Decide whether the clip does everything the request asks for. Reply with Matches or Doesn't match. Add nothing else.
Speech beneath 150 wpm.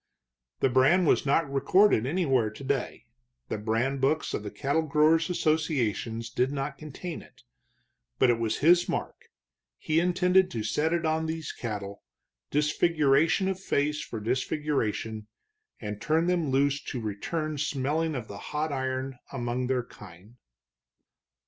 Matches